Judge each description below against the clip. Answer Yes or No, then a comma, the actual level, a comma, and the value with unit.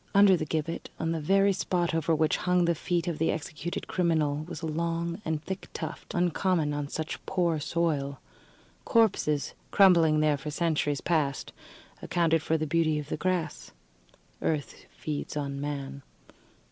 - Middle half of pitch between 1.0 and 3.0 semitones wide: Yes, narrow, 2.4 semitones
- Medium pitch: Yes, medium, 160 Hz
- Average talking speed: Yes, average, 160 wpm